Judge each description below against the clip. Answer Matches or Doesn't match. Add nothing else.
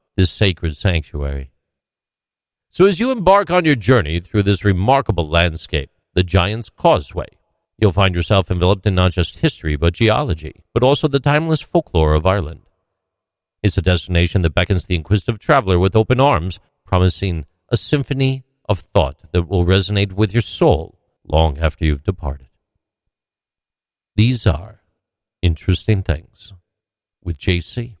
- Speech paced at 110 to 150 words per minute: Matches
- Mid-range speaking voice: Doesn't match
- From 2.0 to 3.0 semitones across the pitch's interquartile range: Doesn't match